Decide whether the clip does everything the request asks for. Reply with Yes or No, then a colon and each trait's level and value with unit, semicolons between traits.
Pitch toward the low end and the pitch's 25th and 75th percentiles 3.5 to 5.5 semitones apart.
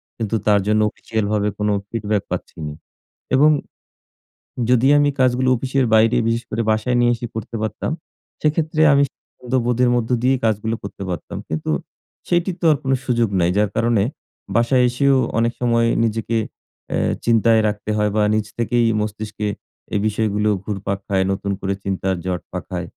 No: low, 115 Hz; average, 2.8 semitones